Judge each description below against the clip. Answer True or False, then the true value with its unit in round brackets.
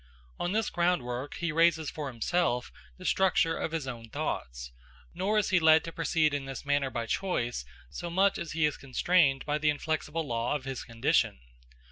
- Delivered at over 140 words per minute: True (185 wpm)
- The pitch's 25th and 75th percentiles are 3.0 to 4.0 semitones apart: False (4.6 semitones)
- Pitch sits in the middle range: True (155 Hz)